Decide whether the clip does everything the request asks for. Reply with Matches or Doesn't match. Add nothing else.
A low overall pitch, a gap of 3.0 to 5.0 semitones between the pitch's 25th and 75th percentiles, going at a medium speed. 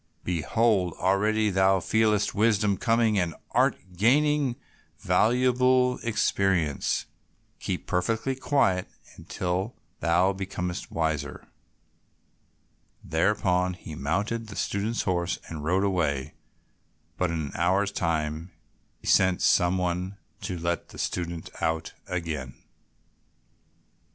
Doesn't match